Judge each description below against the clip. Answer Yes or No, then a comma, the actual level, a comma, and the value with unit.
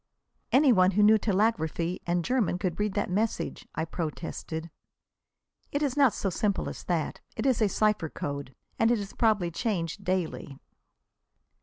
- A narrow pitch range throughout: No, average, 4.6 semitones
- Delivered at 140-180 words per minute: Yes, average, 155 wpm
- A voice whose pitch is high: Yes, high, 195 Hz